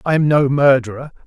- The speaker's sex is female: No, male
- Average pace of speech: Yes, average, 190 wpm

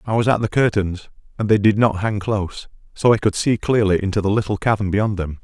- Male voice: Yes, male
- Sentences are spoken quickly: Yes, fast, 245 wpm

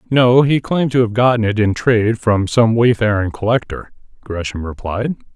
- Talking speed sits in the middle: Yes, average, 170 wpm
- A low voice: Yes, low, 115 Hz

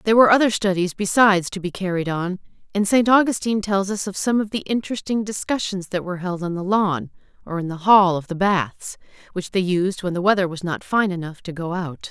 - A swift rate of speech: Yes, fast, 230 wpm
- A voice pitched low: No, high, 190 Hz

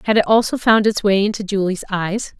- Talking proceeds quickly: Yes, fast, 225 wpm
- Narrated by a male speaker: No, female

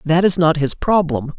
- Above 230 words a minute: No, fast, 215 wpm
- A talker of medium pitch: Yes, medium, 160 Hz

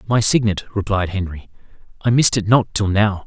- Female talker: No, male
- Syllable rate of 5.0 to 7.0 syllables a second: Yes, 5.5 syllables/s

